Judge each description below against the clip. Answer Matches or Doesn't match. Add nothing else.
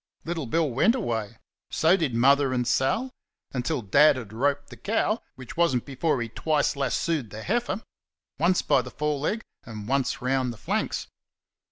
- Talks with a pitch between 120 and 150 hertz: Matches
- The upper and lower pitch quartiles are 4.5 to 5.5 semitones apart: Matches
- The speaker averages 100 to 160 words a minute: Doesn't match